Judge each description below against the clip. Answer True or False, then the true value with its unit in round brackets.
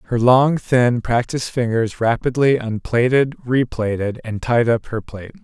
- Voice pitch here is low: True (120 Hz)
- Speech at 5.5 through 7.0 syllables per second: False (4.4 syllables/s)